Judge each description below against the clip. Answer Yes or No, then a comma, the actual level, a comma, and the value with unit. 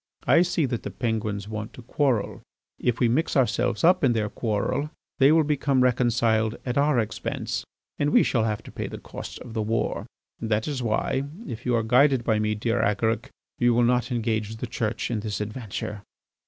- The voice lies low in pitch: Yes, low, 115 Hz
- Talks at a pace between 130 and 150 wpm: No, average, 195 wpm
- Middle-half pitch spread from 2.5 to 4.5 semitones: Yes, average, 2.9 semitones